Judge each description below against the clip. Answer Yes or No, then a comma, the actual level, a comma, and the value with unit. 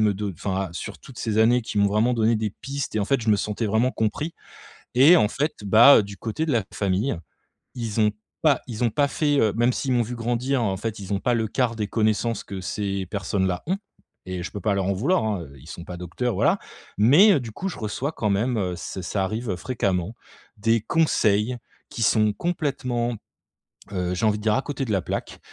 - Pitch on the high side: No, low, 110 Hz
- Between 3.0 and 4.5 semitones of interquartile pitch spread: Yes, average, 3.7 semitones